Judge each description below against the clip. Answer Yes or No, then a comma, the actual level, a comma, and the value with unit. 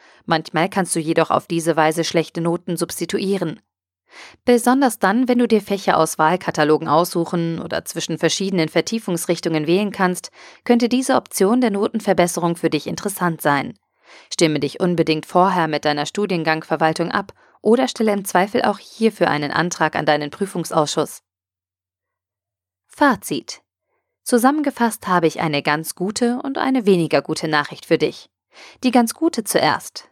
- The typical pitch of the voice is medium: Yes, medium, 175 Hz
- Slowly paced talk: No, average, 140 wpm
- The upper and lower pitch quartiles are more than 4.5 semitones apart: Yes, average, 4.9 semitones